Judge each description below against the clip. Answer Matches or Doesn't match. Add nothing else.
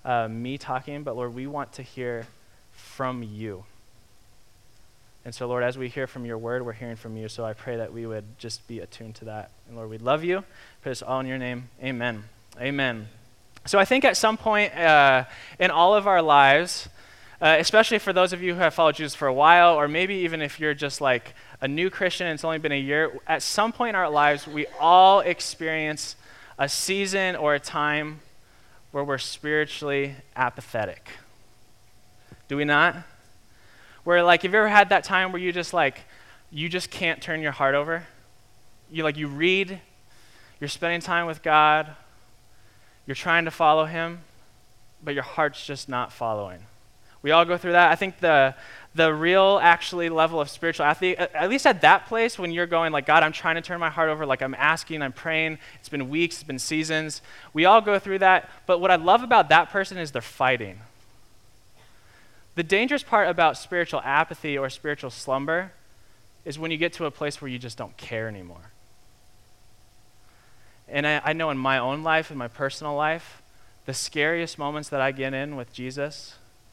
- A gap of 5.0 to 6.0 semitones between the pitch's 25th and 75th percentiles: Matches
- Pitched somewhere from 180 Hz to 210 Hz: Doesn't match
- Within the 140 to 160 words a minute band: Doesn't match